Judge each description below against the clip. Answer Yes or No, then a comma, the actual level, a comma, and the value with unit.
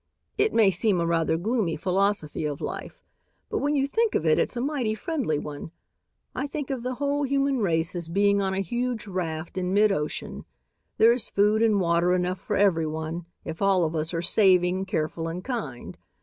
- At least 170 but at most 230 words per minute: Yes, average, 190 wpm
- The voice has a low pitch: No, high, 195 Hz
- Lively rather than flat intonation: Yes, wide, 6.0 semitones